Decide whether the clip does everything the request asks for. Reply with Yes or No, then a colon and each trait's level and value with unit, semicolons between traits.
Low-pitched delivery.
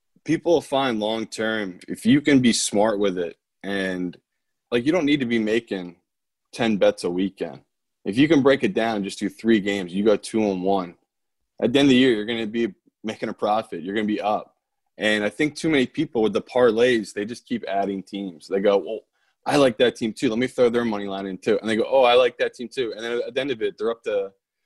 Yes: low, 115 Hz